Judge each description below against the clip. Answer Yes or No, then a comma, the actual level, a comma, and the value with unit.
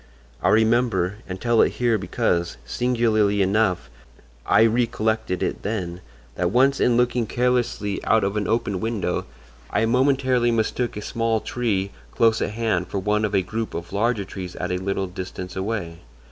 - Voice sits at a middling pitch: No, low, 110 Hz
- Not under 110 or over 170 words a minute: Yes, average, 160 wpm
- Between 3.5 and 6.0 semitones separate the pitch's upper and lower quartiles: Yes, average, 3.8 semitones